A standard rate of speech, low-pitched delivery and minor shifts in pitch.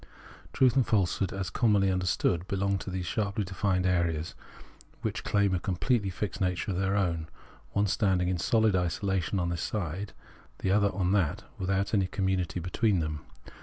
Yes: average, 165 wpm; very low, 95 Hz; narrow, 2.2 semitones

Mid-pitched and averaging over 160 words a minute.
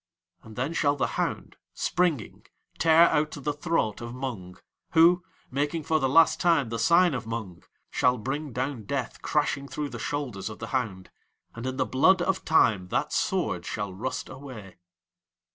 No: low, 130 Hz; average, 170 wpm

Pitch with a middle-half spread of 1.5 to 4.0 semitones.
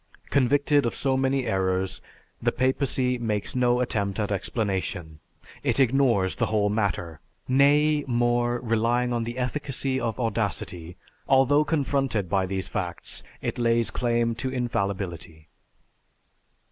No: average, 4.6 semitones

